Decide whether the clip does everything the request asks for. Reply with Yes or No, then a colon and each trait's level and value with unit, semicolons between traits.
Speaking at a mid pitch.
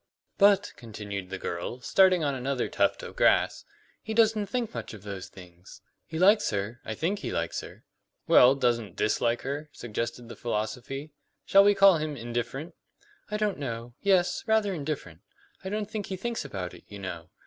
No: low, 130 Hz